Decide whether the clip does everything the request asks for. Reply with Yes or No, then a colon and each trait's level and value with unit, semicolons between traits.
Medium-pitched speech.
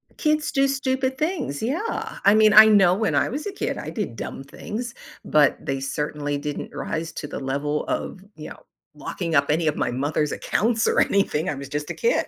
Yes: medium, 175 Hz